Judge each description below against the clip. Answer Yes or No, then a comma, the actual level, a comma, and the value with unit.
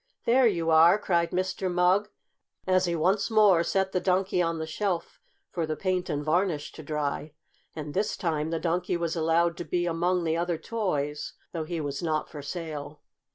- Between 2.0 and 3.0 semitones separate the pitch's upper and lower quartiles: Yes, average, 2.7 semitones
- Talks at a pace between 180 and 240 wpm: Yes, average, 190 wpm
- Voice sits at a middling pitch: Yes, medium, 170 Hz